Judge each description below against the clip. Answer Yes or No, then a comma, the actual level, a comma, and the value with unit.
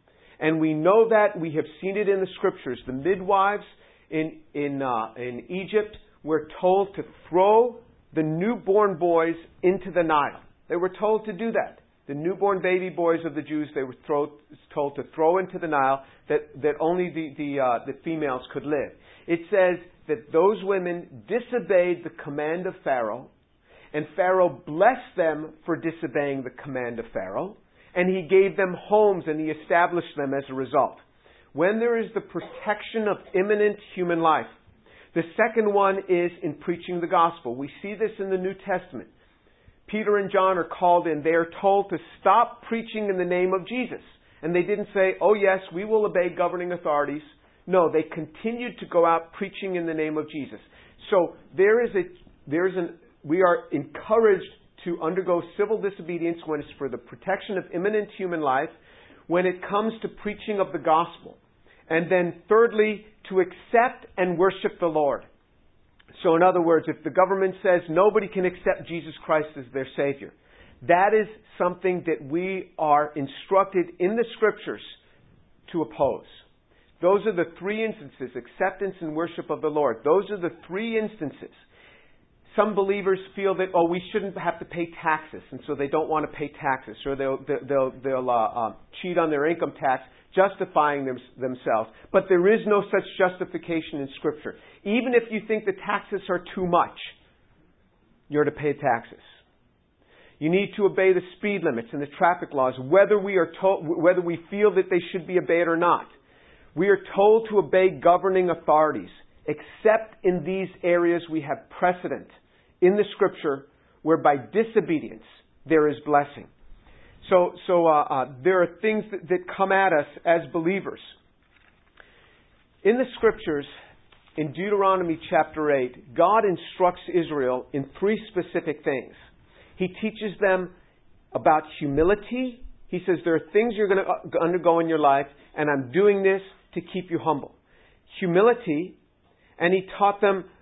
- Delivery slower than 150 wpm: No, average, 170 wpm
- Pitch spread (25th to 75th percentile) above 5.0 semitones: No, average, 4.1 semitones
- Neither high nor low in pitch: Yes, medium, 175 Hz